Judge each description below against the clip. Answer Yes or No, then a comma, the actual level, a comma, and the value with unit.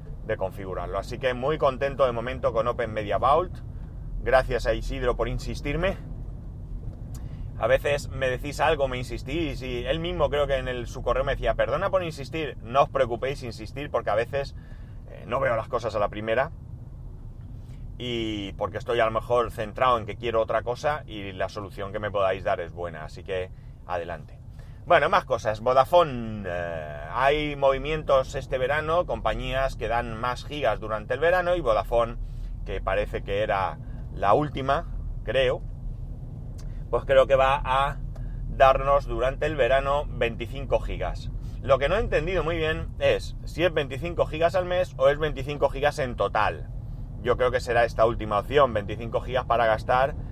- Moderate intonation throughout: Yes, average, 3.8 semitones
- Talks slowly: No, average, 175 wpm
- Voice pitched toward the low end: Yes, low, 125 Hz